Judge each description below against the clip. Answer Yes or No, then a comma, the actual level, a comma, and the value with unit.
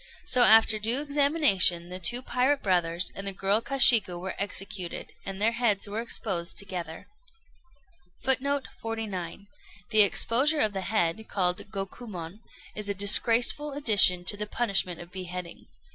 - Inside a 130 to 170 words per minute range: Yes, average, 145 wpm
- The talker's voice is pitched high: Yes, high, 205 Hz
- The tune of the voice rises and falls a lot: No, average, 4.4 semitones